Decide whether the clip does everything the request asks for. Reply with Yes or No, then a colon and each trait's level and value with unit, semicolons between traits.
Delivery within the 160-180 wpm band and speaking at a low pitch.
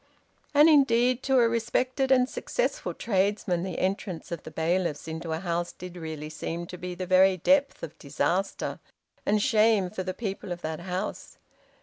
No: average, 175 wpm; medium, 185 Hz